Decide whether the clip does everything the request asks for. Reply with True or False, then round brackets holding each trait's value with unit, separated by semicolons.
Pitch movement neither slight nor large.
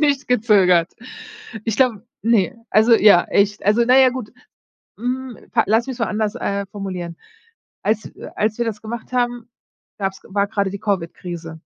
True (3.3 semitones)